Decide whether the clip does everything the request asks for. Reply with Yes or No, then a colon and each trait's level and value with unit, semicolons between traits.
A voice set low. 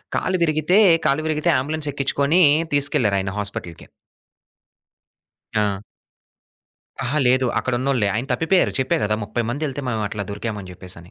Yes: low, 130 Hz